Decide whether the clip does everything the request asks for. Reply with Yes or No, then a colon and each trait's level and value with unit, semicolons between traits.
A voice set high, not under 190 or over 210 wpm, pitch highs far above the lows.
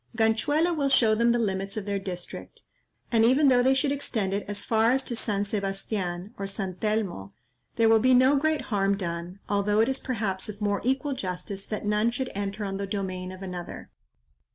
No: high, 210 Hz; average, 200 wpm; average, 3.8 semitones